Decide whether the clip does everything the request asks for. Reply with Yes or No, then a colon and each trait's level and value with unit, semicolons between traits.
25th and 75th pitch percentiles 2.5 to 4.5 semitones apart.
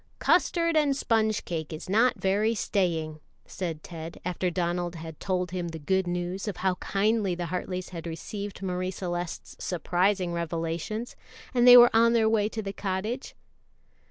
Yes: average, 3.8 semitones